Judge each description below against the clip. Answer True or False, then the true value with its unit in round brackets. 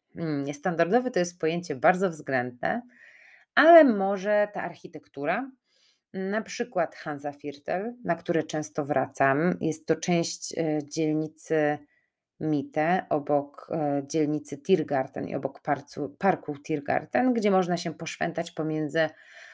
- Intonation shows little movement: False (3.8 semitones)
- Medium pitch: True (160 Hz)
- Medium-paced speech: False (105 wpm)